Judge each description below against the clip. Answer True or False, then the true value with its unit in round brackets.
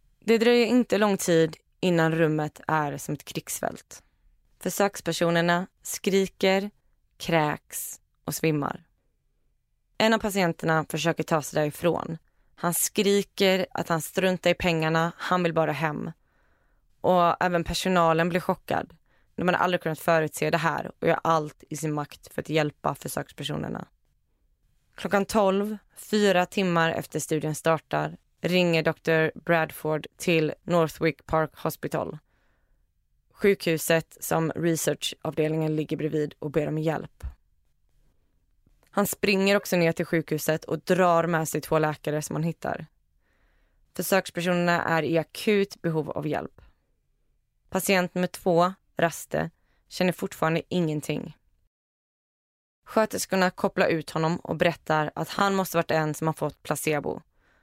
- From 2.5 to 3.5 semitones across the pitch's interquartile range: True (2.8 semitones)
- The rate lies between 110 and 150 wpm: True (130 wpm)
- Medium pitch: True (165 Hz)